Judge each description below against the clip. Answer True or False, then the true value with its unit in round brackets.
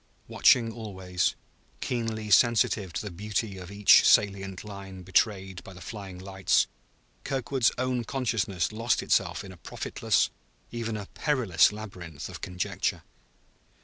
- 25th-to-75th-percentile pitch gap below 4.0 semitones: True (3.3 semitones)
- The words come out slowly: True (130 wpm)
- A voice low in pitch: True (100 Hz)